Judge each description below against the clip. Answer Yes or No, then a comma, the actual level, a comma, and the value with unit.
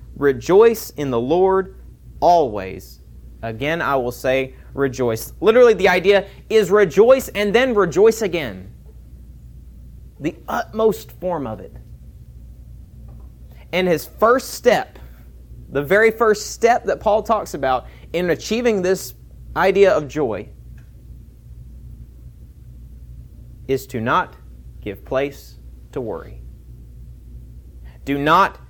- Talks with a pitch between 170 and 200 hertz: No, low, 130 Hz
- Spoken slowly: Yes, slow, 105 wpm